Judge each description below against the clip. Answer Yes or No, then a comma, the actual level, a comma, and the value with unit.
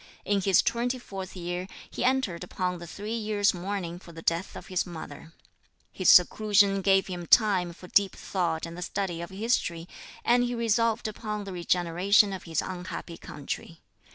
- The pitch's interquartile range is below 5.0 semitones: Yes, average, 3.3 semitones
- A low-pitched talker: No, high, 190 Hz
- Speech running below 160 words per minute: No, average, 175 wpm